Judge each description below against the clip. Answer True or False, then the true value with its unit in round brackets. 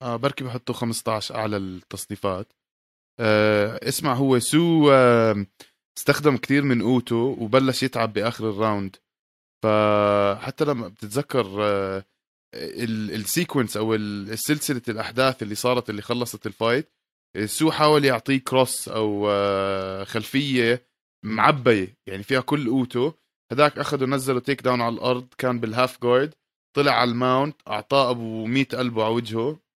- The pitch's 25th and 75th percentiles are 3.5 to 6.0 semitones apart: True (3.8 semitones)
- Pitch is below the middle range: True (120 Hz)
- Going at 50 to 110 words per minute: False (125 wpm)